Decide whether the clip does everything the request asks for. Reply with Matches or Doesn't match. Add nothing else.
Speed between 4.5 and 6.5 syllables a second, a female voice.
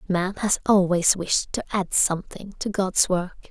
Doesn't match